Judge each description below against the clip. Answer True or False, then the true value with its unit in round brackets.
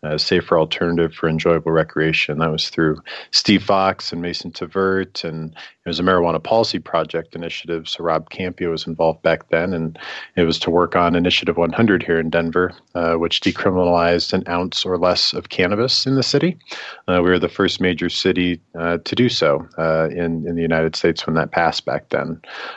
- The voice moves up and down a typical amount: False (1.9 semitones)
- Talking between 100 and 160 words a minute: False (200 wpm)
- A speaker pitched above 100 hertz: False (85 Hz)